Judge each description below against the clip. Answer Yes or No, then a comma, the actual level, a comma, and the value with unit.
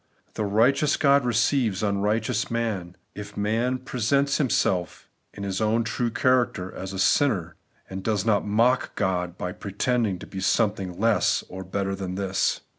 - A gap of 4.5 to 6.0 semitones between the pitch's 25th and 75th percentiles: No, average, 3.9 semitones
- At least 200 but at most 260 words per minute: No, average, 165 wpm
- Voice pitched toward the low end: Yes, low, 105 Hz